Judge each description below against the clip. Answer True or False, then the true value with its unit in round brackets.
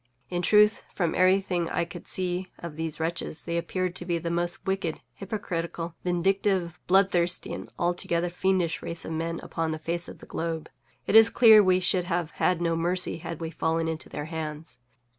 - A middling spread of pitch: False (1.9 semitones)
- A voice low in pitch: False (175 Hz)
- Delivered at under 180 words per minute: False (185 wpm)